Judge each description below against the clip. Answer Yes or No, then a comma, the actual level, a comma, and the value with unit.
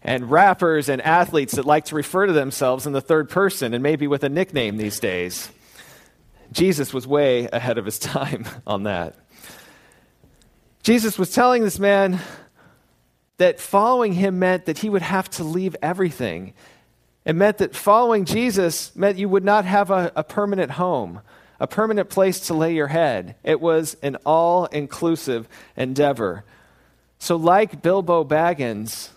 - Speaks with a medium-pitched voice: Yes, medium, 165 Hz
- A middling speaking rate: Yes, average, 160 wpm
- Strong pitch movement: Yes, wide, 5.9 semitones